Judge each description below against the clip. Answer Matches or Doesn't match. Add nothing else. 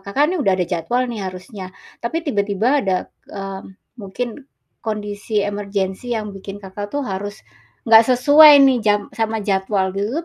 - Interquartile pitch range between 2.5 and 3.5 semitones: Doesn't match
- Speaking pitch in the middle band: Doesn't match